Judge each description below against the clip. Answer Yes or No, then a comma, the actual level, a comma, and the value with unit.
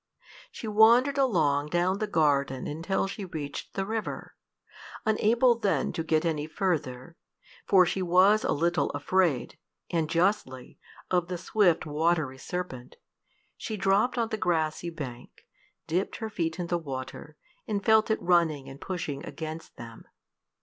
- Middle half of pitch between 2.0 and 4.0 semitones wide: No, average, 4.8 semitones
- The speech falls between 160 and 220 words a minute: No, average, 145 wpm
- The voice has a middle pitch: Yes, medium, 175 Hz